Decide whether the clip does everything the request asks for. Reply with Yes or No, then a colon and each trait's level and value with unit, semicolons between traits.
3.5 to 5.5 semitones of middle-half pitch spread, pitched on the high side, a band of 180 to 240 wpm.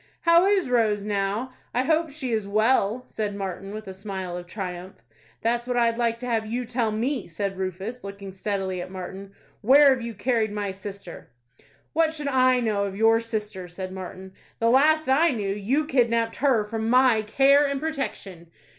Yes: average, 4.5 semitones; high, 220 Hz; average, 185 wpm